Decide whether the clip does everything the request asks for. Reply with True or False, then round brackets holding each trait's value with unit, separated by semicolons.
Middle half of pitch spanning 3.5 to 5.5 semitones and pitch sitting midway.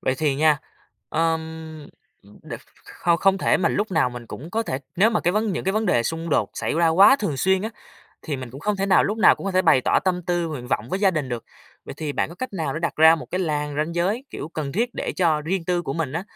True (4.1 semitones; 165 Hz)